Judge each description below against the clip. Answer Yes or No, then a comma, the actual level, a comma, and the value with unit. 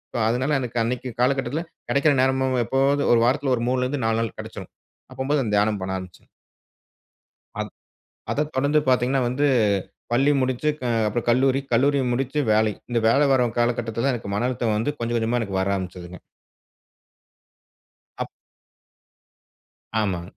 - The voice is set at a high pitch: No, low, 125 Hz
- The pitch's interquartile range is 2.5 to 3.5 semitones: Yes, average, 3.1 semitones